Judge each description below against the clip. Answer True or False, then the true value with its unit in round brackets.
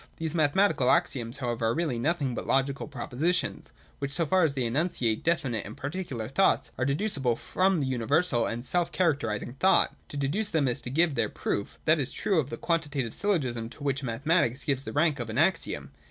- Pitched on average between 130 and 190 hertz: True (140 Hz)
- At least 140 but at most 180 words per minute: False (195 wpm)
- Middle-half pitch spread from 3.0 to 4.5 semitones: False (5.4 semitones)